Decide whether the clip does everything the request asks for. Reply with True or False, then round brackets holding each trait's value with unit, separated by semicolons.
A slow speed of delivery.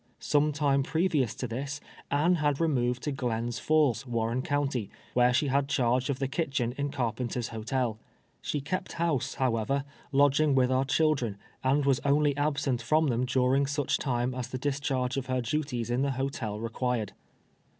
False (170 wpm)